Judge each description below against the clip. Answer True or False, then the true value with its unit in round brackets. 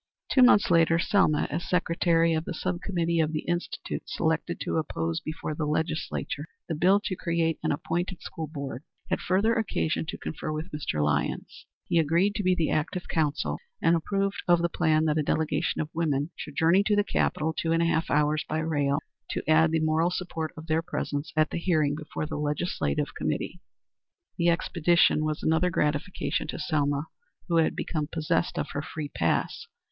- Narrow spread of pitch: True (2.1 semitones)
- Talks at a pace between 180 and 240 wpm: True (190 wpm)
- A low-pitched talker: False (160 Hz)